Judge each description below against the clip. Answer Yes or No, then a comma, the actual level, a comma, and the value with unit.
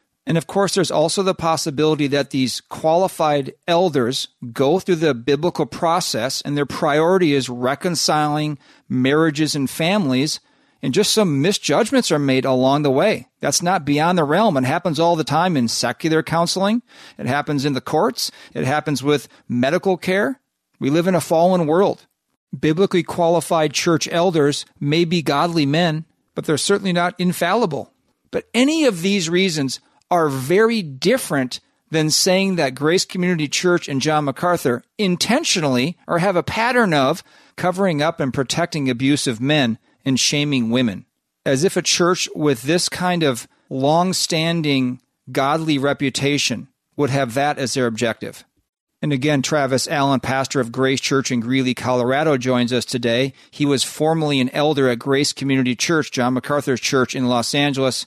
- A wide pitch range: No, average, 4.5 semitones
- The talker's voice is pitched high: No, medium, 150 Hz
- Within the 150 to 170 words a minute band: Yes, average, 160 wpm